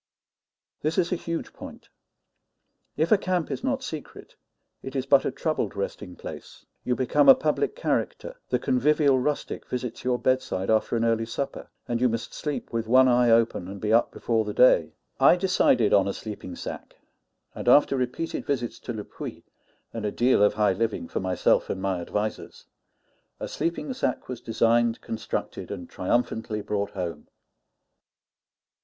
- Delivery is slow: No, average, 170 wpm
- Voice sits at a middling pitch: No, low, 120 Hz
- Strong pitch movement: No, average, 4.7 semitones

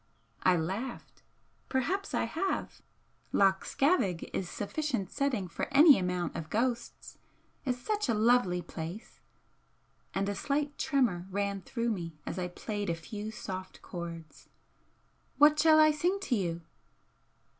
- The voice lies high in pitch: Yes, high, 210 Hz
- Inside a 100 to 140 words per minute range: Yes, slow, 135 wpm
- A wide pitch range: Yes, wide, 7.6 semitones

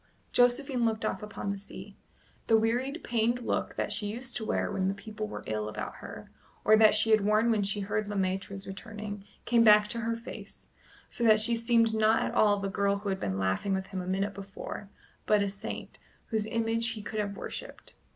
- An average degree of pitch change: No, narrow, 2.3 semitones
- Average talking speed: No, fast, 220 wpm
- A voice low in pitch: No, high, 215 Hz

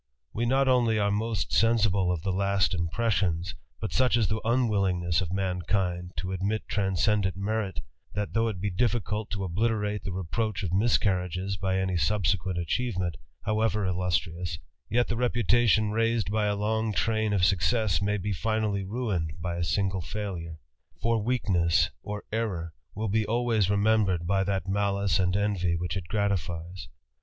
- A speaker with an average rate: Yes, average, 160 wpm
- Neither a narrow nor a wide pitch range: Yes, average, 3.2 semitones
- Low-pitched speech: Yes, low, 100 Hz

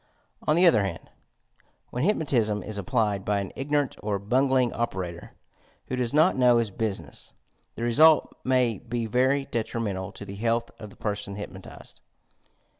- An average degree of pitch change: Yes, average, 4.2 semitones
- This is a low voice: Yes, low, 115 Hz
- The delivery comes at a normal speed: Yes, average, 160 wpm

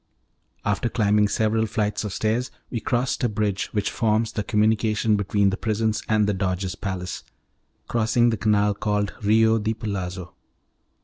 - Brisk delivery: No, average, 160 wpm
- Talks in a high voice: No, low, 105 Hz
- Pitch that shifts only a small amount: Yes, narrow, 1.6 semitones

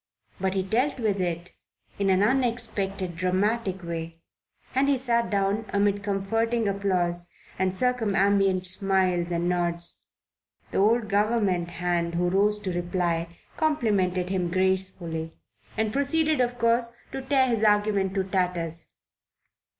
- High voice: Yes, high, 195 Hz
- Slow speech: Yes, slow, 130 wpm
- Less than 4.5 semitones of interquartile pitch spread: Yes, average, 4.0 semitones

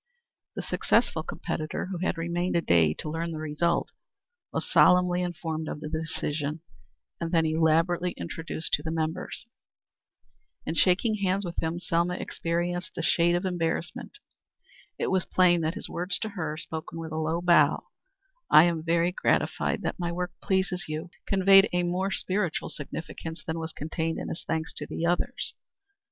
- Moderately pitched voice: Yes, medium, 170 Hz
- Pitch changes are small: Yes, narrow, 1.9 semitones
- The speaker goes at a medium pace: Yes, average, 170 wpm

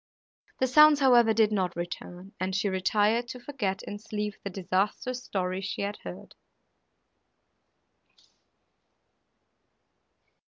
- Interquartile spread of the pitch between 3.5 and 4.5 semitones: Yes, average, 4.1 semitones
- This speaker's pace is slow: Yes, slow, 110 wpm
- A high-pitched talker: Yes, high, 205 Hz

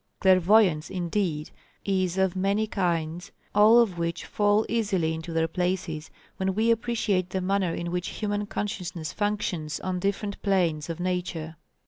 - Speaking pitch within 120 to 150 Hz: No, medium, 185 Hz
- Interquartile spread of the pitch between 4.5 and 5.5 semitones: No, average, 3.4 semitones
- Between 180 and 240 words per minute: No, average, 145 wpm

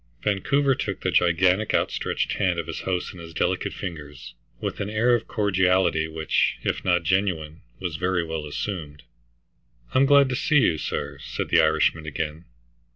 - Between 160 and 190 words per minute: Yes, average, 165 wpm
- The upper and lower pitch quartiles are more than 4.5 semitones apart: No, average, 4.2 semitones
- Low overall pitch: Yes, very low, 90 Hz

